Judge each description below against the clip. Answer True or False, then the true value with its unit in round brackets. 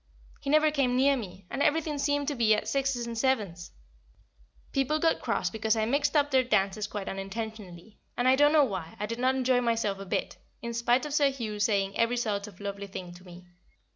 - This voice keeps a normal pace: False (215 wpm)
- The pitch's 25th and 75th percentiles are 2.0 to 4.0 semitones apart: False (5.2 semitones)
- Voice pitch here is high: True (235 Hz)